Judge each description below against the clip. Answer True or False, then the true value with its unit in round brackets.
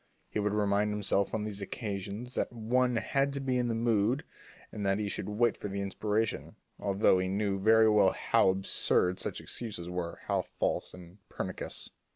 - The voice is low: True (105 Hz)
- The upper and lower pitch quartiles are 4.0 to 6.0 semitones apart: False (2.5 semitones)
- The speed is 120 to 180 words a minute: False (190 wpm)